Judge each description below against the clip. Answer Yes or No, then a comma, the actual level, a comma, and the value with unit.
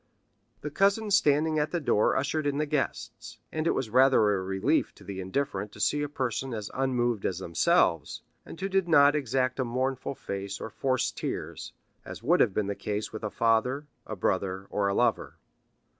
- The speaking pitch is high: No, low, 130 Hz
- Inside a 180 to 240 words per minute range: Yes, average, 195 wpm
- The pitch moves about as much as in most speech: No, wide, 6.0 semitones